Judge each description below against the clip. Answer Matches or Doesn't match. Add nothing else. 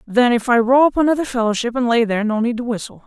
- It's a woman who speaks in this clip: Matches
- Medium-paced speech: Doesn't match